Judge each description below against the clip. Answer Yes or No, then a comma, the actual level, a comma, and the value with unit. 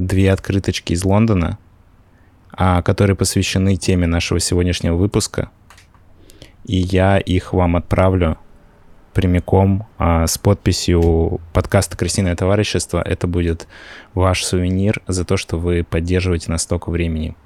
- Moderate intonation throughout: No, narrow, 2.0 semitones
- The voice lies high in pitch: No, very low, 90 Hz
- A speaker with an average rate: Yes, average, 120 wpm